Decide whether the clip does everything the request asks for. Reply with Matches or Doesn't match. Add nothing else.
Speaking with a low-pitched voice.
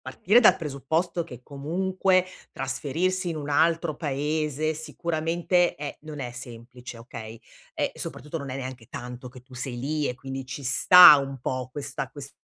Doesn't match